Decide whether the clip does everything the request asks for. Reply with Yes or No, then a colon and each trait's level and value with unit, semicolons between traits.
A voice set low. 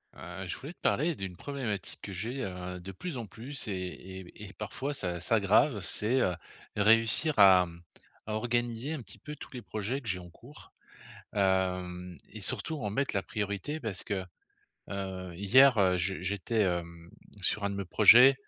Yes: low, 100 Hz